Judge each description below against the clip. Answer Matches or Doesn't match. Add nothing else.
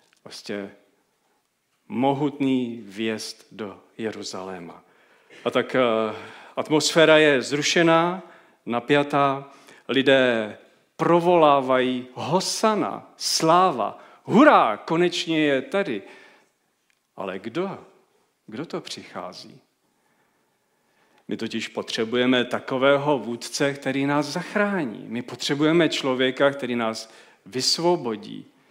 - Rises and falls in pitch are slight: Doesn't match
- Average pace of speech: Doesn't match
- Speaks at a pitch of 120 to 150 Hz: Matches